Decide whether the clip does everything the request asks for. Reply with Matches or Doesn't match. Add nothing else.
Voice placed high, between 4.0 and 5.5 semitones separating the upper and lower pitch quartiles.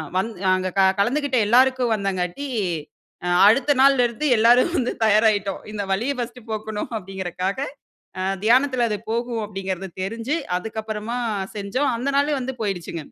Matches